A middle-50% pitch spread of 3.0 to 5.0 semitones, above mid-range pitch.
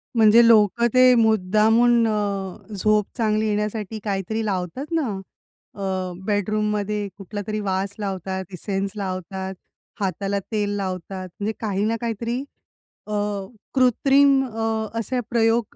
No: narrow, 2.5 semitones; high, 210 Hz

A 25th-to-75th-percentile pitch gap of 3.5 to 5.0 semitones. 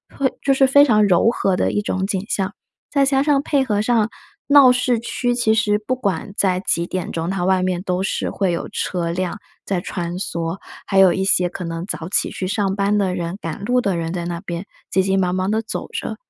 Yes: average, 3.9 semitones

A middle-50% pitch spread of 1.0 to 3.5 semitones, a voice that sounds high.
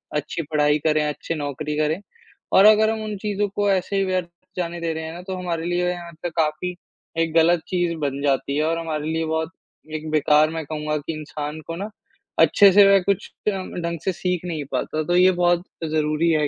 No: average, 2.8 semitones; medium, 165 Hz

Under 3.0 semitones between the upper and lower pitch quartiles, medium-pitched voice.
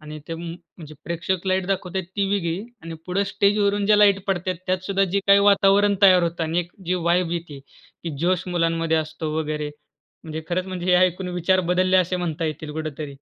Yes: narrow, 2.6 semitones; medium, 175 Hz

